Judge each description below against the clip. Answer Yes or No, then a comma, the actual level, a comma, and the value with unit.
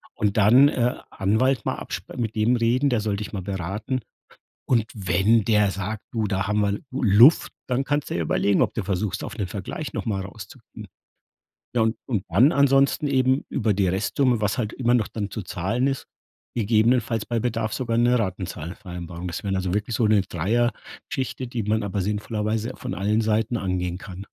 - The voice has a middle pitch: No, low, 110 Hz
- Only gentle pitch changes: No, average, 3.6 semitones